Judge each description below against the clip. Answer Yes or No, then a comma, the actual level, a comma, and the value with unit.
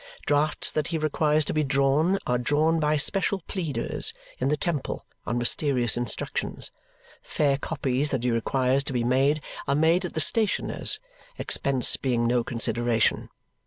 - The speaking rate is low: No, average, 155 wpm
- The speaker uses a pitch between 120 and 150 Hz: Yes, medium, 140 Hz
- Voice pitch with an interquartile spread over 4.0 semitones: No, average, 3.7 semitones